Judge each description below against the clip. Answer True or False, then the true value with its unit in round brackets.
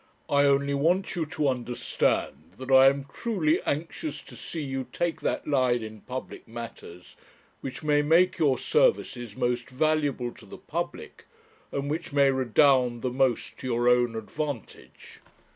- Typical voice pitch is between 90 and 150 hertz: True (135 Hz)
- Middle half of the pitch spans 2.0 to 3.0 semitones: False (3.6 semitones)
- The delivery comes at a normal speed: True (155 wpm)